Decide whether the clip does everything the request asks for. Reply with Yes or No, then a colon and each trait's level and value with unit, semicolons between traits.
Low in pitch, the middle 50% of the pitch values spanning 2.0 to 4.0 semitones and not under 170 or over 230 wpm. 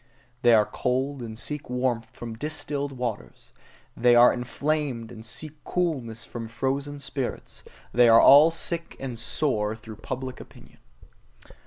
No: low, 125 Hz; average, 3.6 semitones; average, 140 wpm